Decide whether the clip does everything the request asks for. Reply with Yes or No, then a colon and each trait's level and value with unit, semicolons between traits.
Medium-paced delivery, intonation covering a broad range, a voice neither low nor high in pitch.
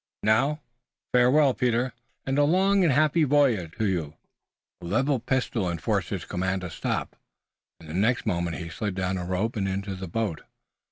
No: average, 175 wpm; wide, 6.6 semitones; low, 110 Hz